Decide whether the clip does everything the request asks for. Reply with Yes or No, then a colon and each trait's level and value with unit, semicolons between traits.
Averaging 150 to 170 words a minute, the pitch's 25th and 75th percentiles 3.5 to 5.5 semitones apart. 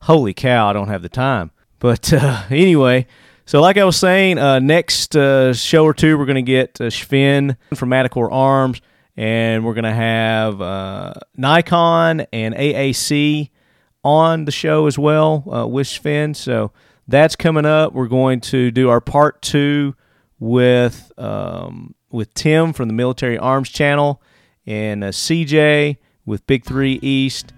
Yes: average, 160 wpm; average, 3.8 semitones